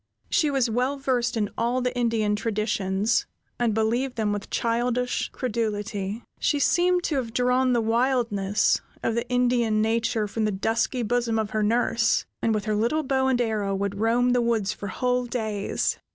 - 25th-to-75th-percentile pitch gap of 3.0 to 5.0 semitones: No, narrow, 2.6 semitones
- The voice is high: Yes, high, 230 Hz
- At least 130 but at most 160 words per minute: No, average, 175 wpm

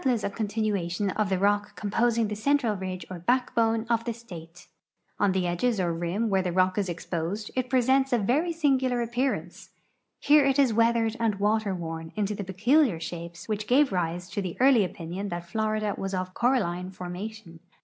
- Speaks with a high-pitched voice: Yes, high, 205 Hz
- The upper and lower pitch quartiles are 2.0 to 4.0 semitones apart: No, average, 4.6 semitones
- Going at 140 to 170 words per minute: No, average, 185 wpm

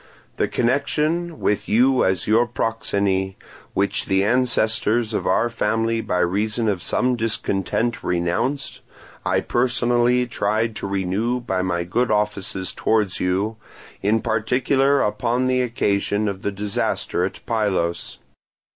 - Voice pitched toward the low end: Yes, low, 110 Hz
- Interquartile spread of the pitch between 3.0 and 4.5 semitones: Yes, average, 3.5 semitones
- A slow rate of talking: Yes, slow, 130 wpm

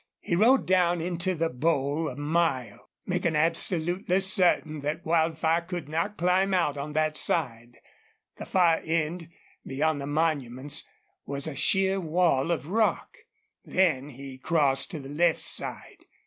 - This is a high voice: No, medium, 160 Hz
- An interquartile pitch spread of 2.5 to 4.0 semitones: Yes, average, 3.3 semitones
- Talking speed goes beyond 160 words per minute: No, average, 145 wpm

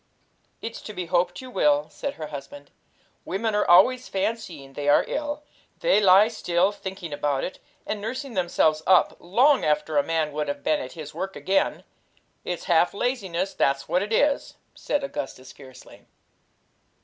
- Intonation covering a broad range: Yes, wide, 6.1 semitones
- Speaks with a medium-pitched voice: Yes, medium, 180 Hz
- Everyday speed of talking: Yes, average, 165 wpm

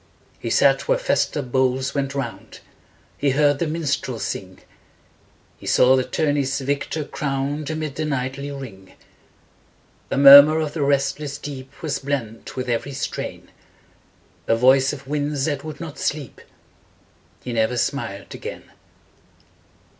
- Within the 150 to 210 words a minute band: No, average, 140 wpm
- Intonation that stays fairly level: Yes, narrow, 2.0 semitones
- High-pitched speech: No, medium, 140 Hz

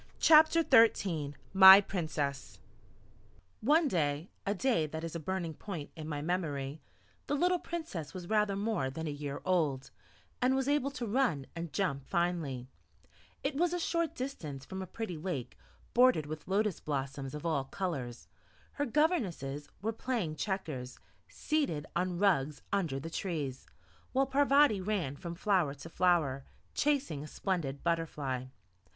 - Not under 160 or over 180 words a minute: No, average, 150 wpm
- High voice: No, medium, 175 Hz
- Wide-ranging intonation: Yes, wide, 7.5 semitones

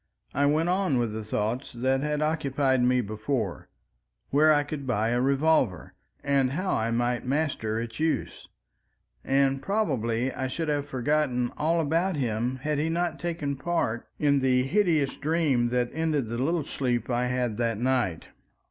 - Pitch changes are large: No, average, 4.2 semitones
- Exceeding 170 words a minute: No, average, 160 wpm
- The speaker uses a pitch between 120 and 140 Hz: Yes, low, 135 Hz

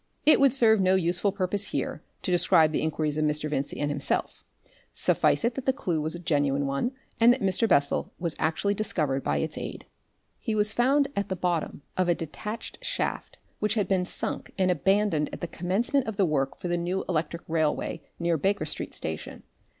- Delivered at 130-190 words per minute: No, average, 200 wpm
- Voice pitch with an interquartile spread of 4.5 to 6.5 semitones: Yes, average, 5.1 semitones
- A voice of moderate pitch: Yes, medium, 180 Hz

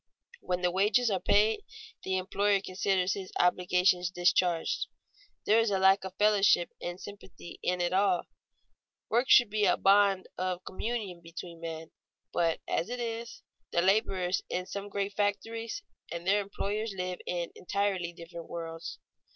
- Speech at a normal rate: Yes, average, 150 wpm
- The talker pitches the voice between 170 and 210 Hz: Yes, high, 190 Hz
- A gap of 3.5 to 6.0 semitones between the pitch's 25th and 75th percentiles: No, narrow, 2.4 semitones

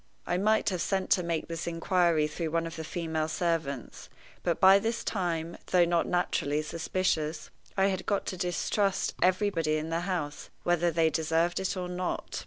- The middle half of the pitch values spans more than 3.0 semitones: No, narrow, 2.4 semitones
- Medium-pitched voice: Yes, medium, 170 Hz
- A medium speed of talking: Yes, average, 180 wpm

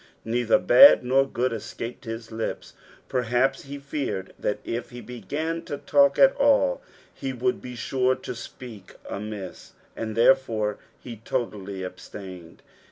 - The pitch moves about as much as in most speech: Yes, average, 3.8 semitones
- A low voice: Yes, low, 120 Hz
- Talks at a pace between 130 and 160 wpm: Yes, average, 140 wpm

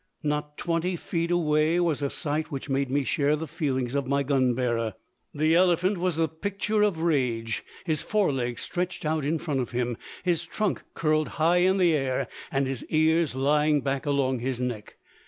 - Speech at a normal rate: Yes, average, 185 wpm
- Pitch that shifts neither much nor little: Yes, average, 3.9 semitones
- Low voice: No, medium, 150 Hz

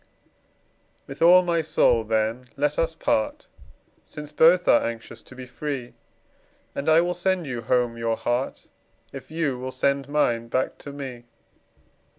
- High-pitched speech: No, medium, 140 Hz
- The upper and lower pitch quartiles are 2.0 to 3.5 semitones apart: No, average, 5.1 semitones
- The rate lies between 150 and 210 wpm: Yes, average, 155 wpm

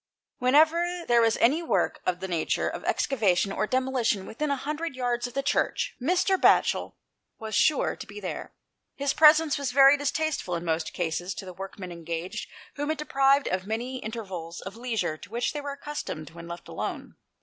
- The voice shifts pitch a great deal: Yes, wide, 7.2 semitones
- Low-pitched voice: No, high, 240 Hz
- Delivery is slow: No, average, 185 wpm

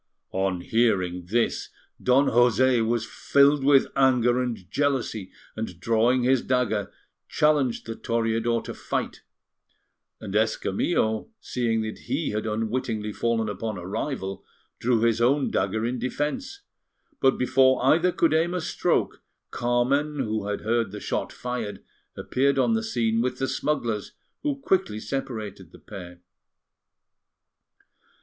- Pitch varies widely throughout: No, average, 3.6 semitones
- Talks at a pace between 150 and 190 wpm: No, slow, 135 wpm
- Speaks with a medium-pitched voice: No, low, 120 Hz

